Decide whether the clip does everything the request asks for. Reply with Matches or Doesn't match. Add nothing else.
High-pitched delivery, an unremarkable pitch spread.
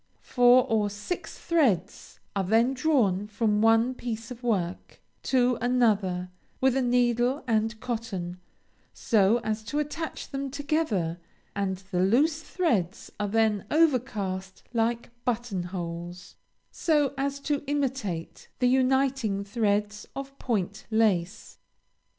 Matches